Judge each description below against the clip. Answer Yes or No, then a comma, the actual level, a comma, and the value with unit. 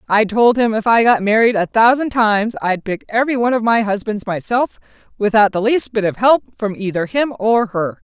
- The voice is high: Yes, high, 220 Hz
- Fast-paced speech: Yes, fast, 215 wpm